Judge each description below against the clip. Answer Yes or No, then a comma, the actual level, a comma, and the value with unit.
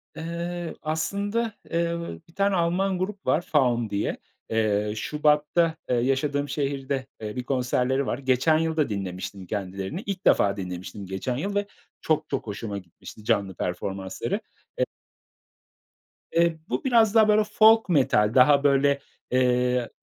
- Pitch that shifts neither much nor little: No, wide, 7.9 semitones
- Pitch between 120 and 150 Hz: Yes, medium, 140 Hz